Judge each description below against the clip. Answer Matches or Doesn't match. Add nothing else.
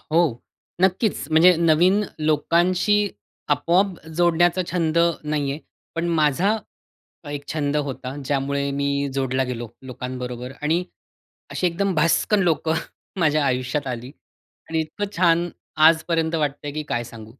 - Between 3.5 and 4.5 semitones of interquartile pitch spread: Matches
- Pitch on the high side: Doesn't match